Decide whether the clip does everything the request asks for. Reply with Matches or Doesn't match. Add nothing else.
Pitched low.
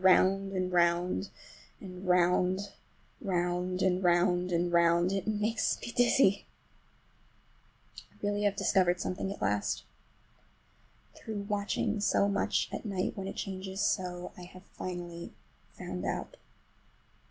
Doesn't match